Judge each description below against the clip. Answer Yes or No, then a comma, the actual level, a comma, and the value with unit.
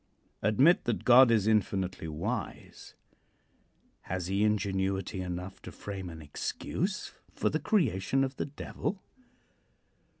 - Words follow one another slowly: Yes, slow, 120 wpm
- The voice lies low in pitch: Yes, low, 100 Hz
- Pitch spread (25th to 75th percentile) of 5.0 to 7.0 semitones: Yes, average, 5.3 semitones